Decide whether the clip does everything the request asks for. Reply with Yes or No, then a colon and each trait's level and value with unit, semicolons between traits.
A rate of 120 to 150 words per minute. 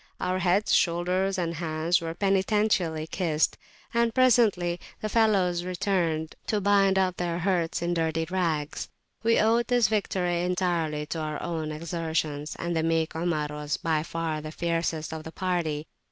No: average, 160 wpm